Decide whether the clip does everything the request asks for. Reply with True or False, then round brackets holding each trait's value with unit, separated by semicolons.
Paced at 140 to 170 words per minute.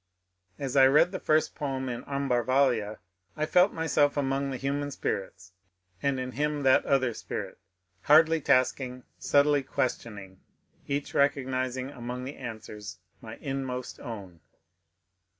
True (150 wpm)